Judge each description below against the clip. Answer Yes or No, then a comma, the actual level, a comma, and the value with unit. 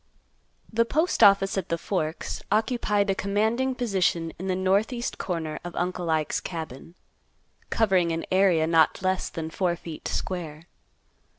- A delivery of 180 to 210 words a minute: No, slow, 135 wpm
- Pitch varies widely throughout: No, average, 3.6 semitones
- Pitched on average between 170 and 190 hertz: Yes, medium, 185 Hz